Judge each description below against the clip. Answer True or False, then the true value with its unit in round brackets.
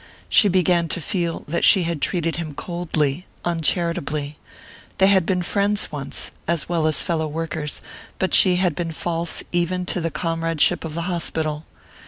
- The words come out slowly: False (165 wpm)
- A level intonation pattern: True (2.1 semitones)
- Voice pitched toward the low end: False (170 Hz)